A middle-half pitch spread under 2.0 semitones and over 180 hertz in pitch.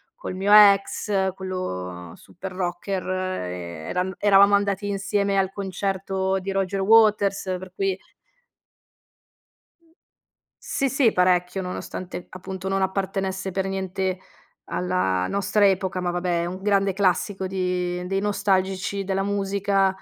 Yes: narrow, 1.3 semitones; high, 190 Hz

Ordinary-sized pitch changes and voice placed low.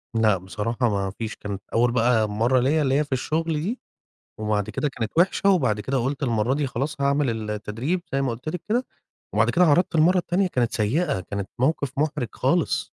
No: wide, 5.7 semitones; low, 130 Hz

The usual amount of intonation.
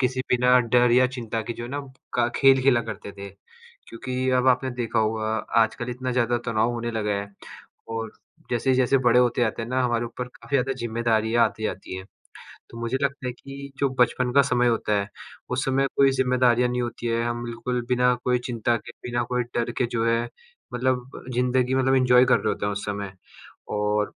No: narrow, 1.7 semitones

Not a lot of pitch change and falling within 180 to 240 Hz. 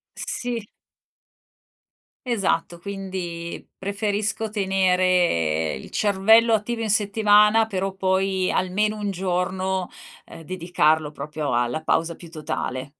No: average, 3.6 semitones; high, 190 Hz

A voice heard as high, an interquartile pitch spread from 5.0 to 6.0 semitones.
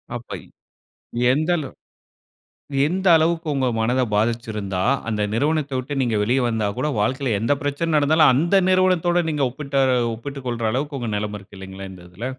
No: low, 130 Hz; wide, 5.5 semitones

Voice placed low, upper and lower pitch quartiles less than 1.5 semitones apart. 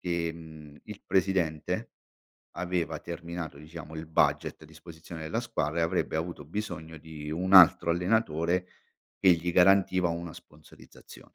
No: very low, 85 Hz; narrow, 2.1 semitones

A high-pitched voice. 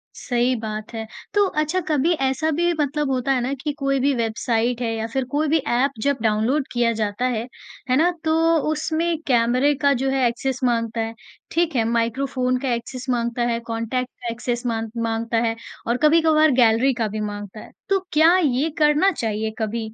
Yes: very high, 250 Hz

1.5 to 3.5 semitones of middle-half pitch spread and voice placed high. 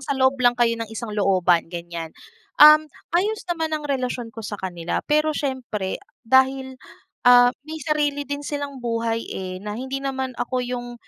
No: average, 4.3 semitones; very high, 250 Hz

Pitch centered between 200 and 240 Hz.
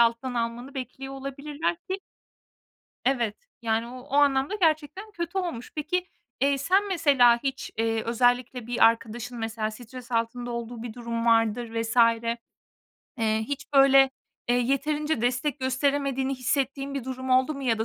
No: very high, 255 Hz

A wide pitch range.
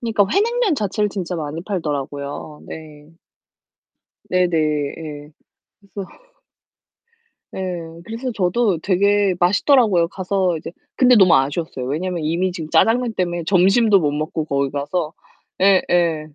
No: average, 4.6 semitones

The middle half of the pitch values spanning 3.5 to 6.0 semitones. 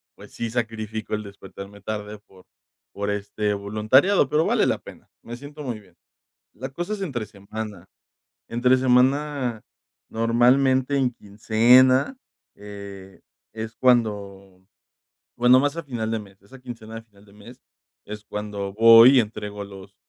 Yes: average, 3.9 semitones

